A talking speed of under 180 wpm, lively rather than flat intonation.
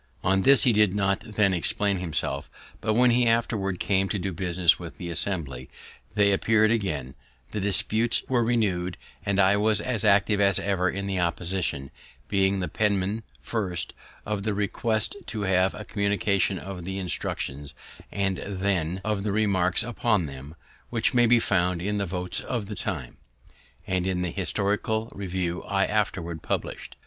No: average, 165 wpm; average, 2.8 semitones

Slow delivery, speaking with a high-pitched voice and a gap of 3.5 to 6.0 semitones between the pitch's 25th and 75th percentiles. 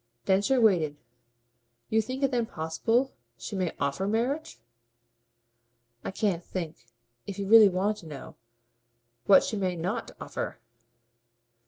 Yes: slow, 130 wpm; high, 195 Hz; average, 4.9 semitones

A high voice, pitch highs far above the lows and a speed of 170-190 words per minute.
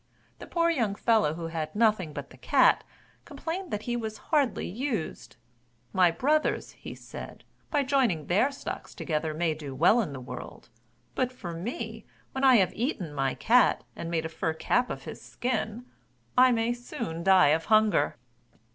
Yes: high, 215 Hz; wide, 7.3 semitones; average, 175 wpm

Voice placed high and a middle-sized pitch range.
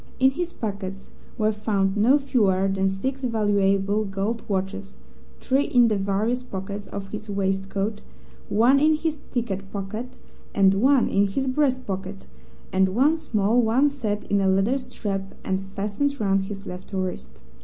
Yes: high, 205 Hz; average, 4.2 semitones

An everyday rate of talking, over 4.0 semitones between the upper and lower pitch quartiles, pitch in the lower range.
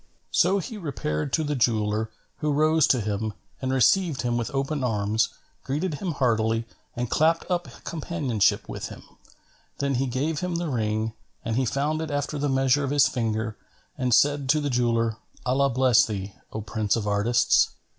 Yes: average, 175 wpm; average, 4.7 semitones; low, 130 Hz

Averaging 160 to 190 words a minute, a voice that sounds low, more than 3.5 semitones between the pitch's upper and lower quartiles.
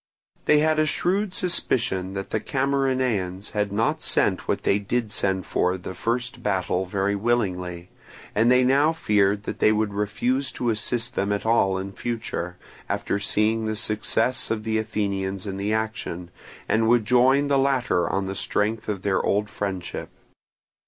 Yes: average, 165 wpm; low, 110 Hz; average, 3.9 semitones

